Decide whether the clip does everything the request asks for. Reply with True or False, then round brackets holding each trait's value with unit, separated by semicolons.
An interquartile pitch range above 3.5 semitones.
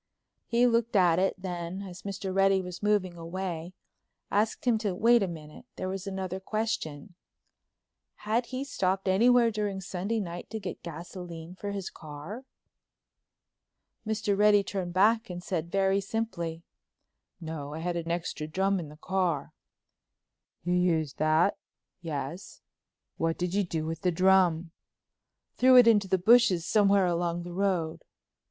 False (3.2 semitones)